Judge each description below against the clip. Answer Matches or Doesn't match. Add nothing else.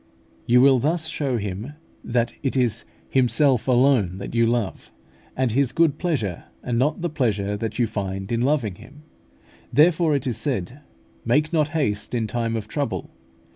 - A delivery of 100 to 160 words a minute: Doesn't match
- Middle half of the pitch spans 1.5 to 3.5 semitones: Doesn't match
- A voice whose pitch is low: Matches